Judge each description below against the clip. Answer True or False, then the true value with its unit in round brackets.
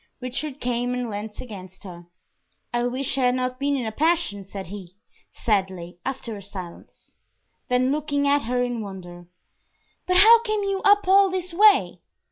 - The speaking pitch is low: False (250 Hz)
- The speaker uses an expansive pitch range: True (7.0 semitones)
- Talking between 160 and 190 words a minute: True (170 wpm)